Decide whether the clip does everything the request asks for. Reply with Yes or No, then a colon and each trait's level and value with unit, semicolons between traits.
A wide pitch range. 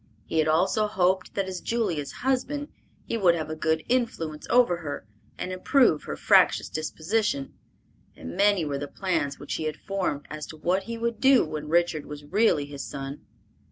Yes: wide, 5.7 semitones